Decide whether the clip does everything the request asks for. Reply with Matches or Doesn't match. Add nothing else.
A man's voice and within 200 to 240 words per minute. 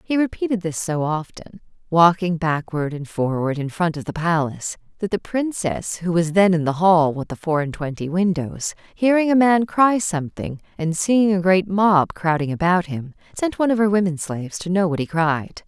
Doesn't match